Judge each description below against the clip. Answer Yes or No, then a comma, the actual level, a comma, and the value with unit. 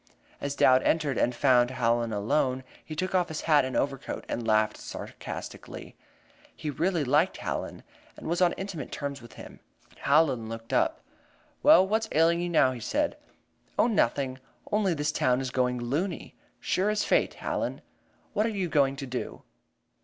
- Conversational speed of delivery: Yes, average, 170 wpm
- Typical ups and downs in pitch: No, wide, 5.7 semitones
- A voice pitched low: No, medium, 145 Hz